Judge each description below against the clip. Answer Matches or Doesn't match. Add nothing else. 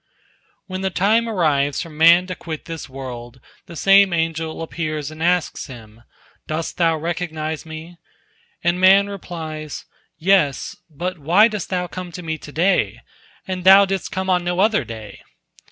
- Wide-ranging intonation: Doesn't match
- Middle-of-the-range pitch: Matches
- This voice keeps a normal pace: Matches